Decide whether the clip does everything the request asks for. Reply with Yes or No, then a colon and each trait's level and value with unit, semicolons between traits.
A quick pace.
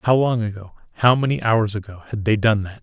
Yes: fast, 235 wpm